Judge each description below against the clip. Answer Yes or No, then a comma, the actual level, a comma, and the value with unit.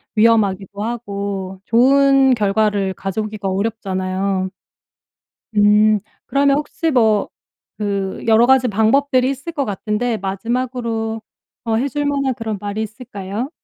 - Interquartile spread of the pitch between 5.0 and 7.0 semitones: No, average, 4.0 semitones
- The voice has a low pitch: No, high, 220 Hz